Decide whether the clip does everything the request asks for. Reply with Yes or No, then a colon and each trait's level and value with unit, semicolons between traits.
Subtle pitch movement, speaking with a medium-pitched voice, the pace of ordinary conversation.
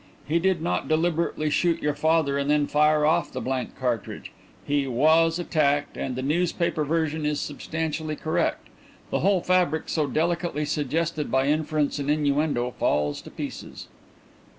Yes: narrow, 2.3 semitones; medium, 155 Hz; average, 150 wpm